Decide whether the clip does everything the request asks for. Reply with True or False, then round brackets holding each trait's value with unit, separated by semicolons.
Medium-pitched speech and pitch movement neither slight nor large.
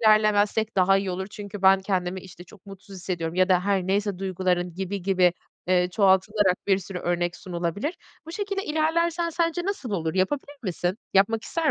False (195 Hz; 3.1 semitones)